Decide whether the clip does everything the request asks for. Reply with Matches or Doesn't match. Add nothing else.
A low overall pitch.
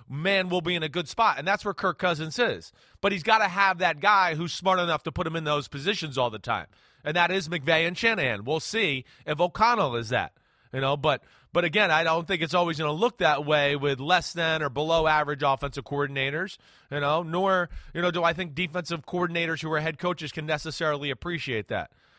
Doesn't match